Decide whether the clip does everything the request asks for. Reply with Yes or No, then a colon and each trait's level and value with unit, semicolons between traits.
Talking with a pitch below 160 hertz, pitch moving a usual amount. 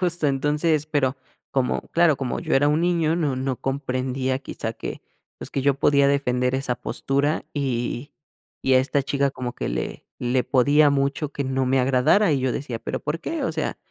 No: medium, 140 Hz; narrow, 2.3 semitones